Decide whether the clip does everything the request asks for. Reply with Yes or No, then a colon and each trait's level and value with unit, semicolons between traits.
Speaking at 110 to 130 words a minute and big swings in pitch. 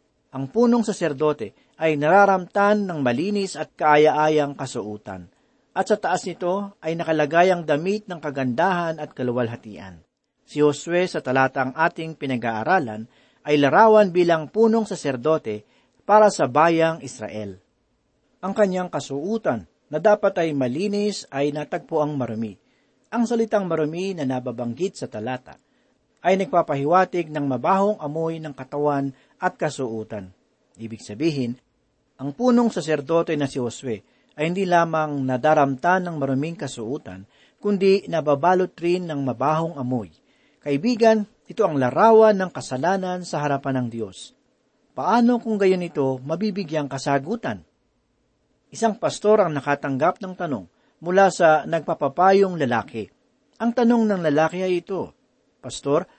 Yes: average, 125 wpm; wide, 5.9 semitones